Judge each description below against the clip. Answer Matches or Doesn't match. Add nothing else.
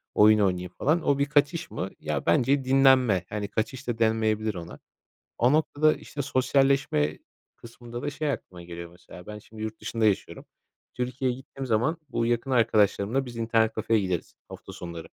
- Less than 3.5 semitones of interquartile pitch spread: Doesn't match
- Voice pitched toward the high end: Doesn't match